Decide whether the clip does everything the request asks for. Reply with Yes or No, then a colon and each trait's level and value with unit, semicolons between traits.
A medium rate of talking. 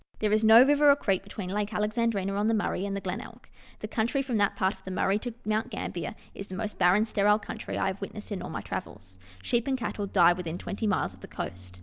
No: fast, 250 wpm